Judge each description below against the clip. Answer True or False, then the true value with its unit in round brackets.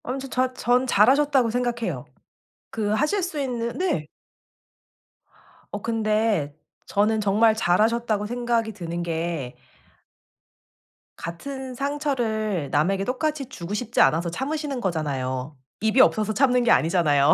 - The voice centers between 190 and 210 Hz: False (220 Hz)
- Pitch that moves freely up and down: True (6.5 semitones)